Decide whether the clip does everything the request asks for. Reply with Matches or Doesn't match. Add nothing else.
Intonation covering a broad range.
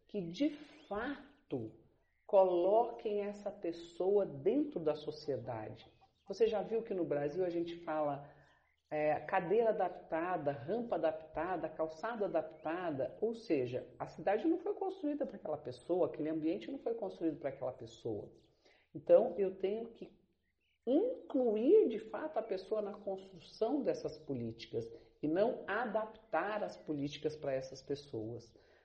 Matches